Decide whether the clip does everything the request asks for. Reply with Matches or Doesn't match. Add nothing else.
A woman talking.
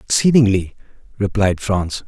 Doesn't match